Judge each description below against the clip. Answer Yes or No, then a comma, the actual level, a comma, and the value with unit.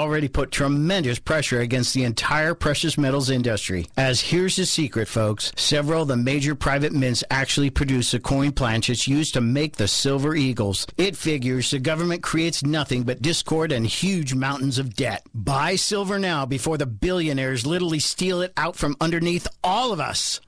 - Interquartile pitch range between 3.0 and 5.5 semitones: Yes, average, 3.9 semitones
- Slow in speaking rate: No, average, 175 wpm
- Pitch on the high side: No, medium, 140 Hz